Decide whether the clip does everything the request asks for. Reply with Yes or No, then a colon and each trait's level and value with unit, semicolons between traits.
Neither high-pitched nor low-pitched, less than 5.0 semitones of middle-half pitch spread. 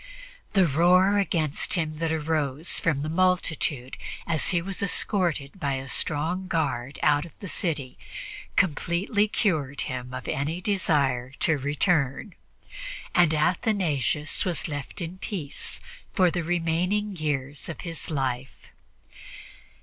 Yes: medium, 160 Hz; average, 4.2 semitones